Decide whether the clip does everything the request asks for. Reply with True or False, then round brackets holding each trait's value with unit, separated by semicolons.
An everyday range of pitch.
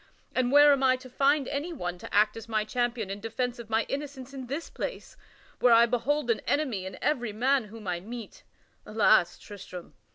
True (4.2 semitones)